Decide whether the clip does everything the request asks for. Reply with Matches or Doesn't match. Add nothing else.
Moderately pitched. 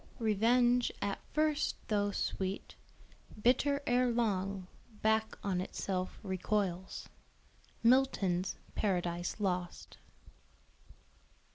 Doesn't match